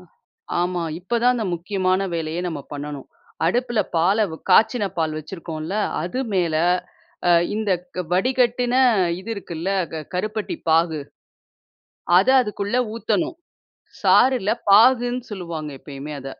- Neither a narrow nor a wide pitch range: No, wide, 5.9 semitones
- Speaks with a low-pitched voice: No, medium, 185 Hz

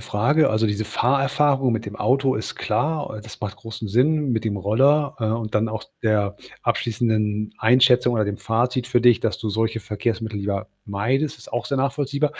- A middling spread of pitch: Yes, average, 3.7 semitones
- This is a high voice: No, low, 115 Hz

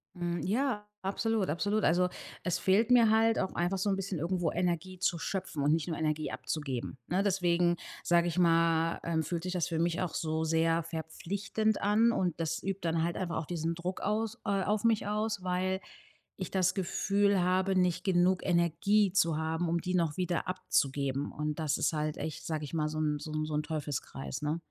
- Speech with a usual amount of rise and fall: Yes, average, 3.2 semitones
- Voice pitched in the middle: Yes, medium, 175 Hz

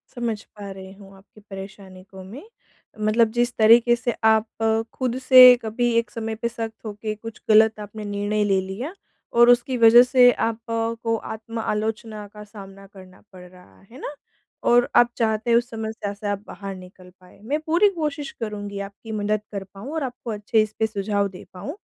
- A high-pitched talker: Yes, high, 220 Hz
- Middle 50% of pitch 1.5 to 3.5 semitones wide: Yes, average, 2.8 semitones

